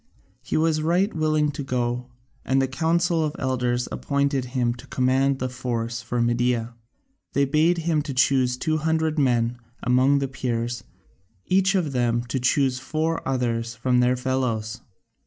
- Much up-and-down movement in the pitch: No, average, 3.9 semitones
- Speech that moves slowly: No, average, 155 wpm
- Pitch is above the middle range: No, low, 130 Hz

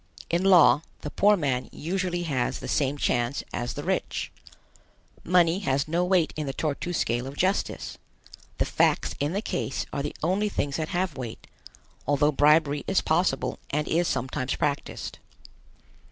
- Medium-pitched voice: Yes, medium, 150 Hz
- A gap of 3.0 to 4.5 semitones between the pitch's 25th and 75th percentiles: Yes, average, 4.1 semitones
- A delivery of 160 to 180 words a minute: Yes, average, 165 wpm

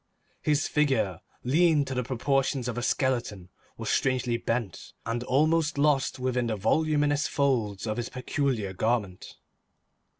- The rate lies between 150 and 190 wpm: No, slow, 135 wpm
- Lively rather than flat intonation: No, average, 3.8 semitones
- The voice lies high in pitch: No, low, 125 Hz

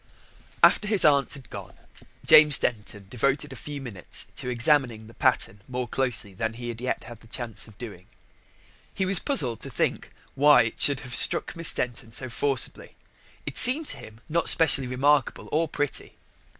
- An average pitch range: Yes, average, 4.4 semitones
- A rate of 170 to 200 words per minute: Yes, average, 175 wpm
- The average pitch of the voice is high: No, low, 125 Hz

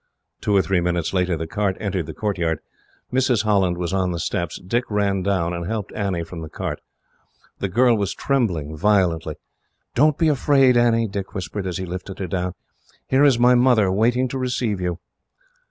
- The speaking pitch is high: No, low, 100 Hz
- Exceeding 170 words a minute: Yes, average, 185 wpm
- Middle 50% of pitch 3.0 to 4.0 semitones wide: No, average, 4.9 semitones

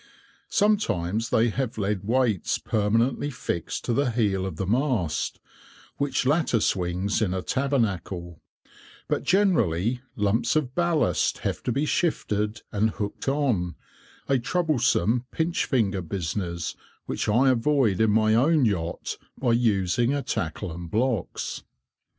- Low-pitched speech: Yes, low, 115 Hz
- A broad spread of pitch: Yes, wide, 5.7 semitones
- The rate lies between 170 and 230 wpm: No, slow, 135 wpm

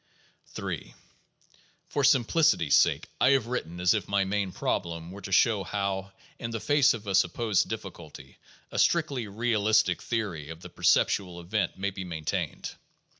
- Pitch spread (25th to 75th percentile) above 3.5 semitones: Yes, average, 4.3 semitones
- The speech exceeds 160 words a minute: No, average, 155 wpm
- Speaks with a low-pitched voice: Yes, low, 100 Hz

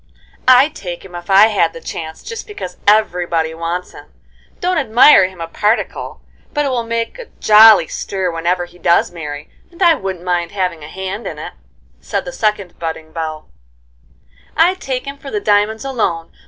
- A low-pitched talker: No, high, 190 Hz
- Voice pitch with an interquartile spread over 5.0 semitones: Yes, wide, 5.5 semitones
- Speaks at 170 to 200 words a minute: Yes, average, 180 wpm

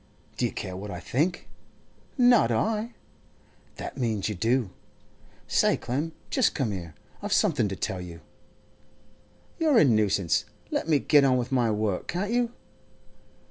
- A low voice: Yes, low, 125 Hz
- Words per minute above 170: No, average, 150 wpm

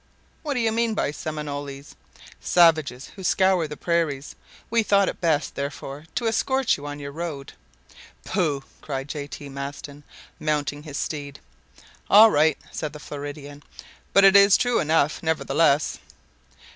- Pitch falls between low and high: Yes, medium, 150 Hz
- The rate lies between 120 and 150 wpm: Yes, average, 145 wpm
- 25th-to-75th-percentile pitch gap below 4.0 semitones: No, average, 4.8 semitones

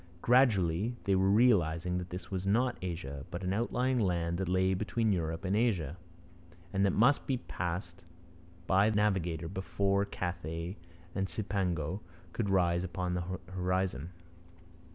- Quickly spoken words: No, average, 145 wpm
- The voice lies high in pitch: No, very low, 95 Hz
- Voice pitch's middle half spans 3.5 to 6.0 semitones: No, narrow, 2.6 semitones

